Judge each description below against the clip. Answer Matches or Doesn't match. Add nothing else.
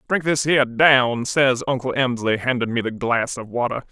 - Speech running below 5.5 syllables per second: Matches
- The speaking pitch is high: Doesn't match